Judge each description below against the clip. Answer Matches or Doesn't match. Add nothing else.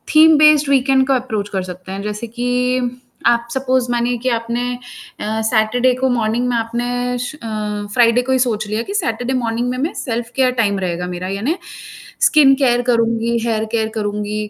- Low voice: Doesn't match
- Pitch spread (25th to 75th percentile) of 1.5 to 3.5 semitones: Matches